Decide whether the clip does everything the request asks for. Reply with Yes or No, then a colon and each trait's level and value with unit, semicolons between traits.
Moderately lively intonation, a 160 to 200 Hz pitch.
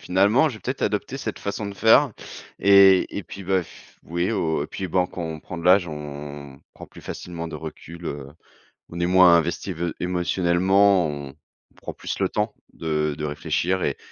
No: average, 3.5 semitones; very low, 90 Hz